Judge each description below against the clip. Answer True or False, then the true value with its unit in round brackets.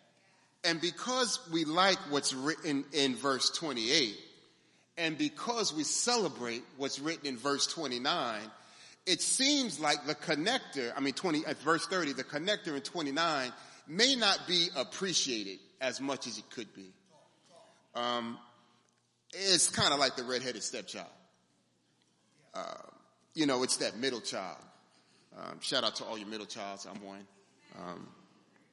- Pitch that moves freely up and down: True (6.0 semitones)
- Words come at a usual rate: True (145 wpm)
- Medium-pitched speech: True (145 Hz)